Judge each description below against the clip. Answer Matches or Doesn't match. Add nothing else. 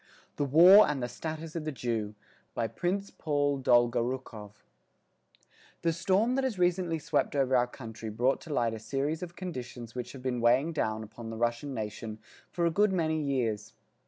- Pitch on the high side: Doesn't match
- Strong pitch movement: Matches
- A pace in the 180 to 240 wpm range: Matches